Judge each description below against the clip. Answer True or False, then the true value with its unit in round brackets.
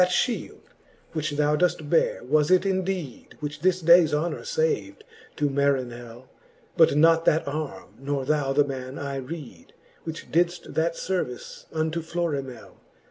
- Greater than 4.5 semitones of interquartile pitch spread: False (3.7 semitones)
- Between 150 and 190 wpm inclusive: False (140 wpm)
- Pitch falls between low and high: True (155 Hz)